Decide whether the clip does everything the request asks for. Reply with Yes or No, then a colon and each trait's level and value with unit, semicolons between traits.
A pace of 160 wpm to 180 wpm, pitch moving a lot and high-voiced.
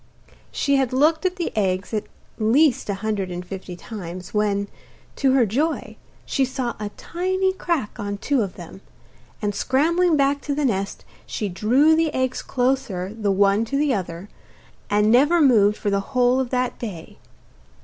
Yes: average, 170 wpm; wide, 5.8 semitones; high, 240 Hz